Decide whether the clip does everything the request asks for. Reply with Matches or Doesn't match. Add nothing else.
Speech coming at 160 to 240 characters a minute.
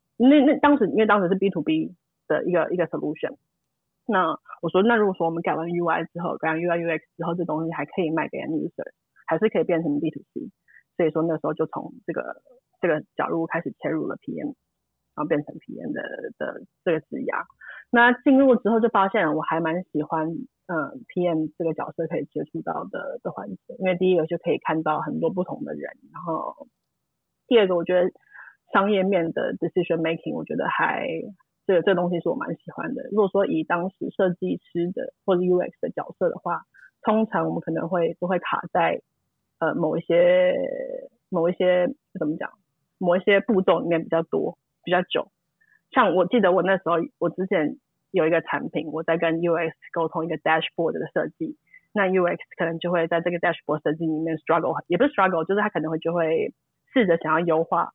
Doesn't match